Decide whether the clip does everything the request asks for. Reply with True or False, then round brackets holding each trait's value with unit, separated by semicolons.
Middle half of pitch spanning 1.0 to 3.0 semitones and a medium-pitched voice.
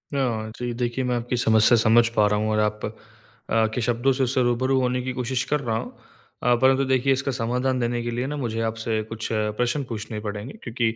False (2.5 semitones; 120 Hz)